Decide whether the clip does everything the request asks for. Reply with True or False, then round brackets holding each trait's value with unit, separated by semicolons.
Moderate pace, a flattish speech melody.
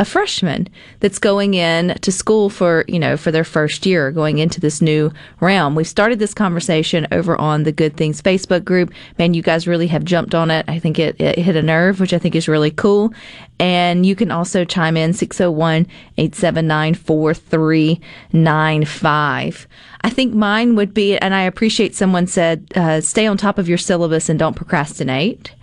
False (185 wpm; 3.2 semitones)